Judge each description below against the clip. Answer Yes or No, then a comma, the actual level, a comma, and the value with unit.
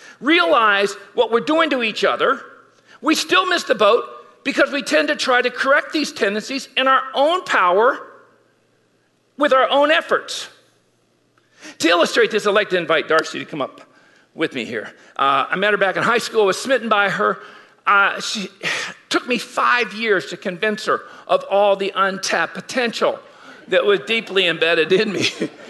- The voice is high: Yes, high, 235 Hz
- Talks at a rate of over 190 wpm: No, average, 175 wpm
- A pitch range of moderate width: No, wide, 6.6 semitones